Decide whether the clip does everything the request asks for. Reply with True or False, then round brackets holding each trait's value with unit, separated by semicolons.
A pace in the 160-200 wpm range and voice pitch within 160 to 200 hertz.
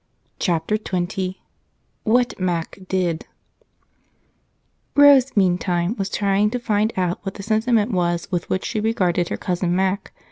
False (135 wpm; 190 Hz)